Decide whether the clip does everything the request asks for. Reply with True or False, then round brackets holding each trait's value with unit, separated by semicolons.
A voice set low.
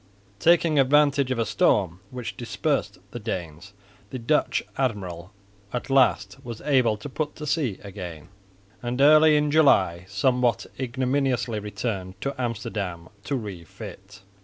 True (120 Hz)